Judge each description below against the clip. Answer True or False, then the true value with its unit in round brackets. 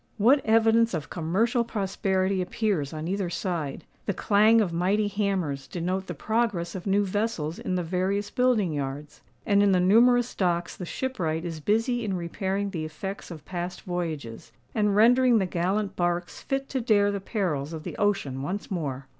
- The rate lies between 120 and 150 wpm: False (175 wpm)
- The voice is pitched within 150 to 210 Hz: True (190 Hz)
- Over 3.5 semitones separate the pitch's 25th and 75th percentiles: True (3.9 semitones)